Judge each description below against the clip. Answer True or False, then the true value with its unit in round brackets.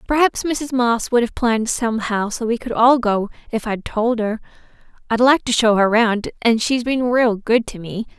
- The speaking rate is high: True (215 wpm)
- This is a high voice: True (230 Hz)